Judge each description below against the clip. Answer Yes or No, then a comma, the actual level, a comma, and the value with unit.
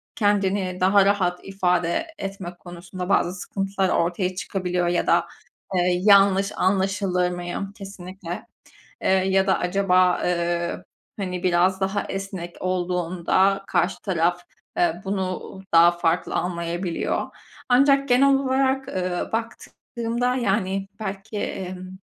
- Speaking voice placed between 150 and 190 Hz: Yes, medium, 185 Hz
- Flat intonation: Yes, narrow, 1.9 semitones